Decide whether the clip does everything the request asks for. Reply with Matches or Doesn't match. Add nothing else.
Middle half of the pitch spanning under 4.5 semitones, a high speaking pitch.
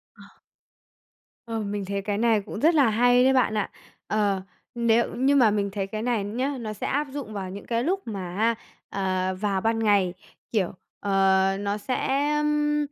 Matches